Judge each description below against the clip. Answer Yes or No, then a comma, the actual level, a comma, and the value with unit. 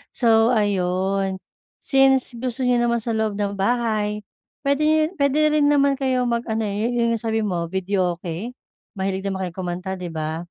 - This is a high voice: Yes, high, 215 Hz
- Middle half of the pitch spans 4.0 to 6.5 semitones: Yes, average, 4.3 semitones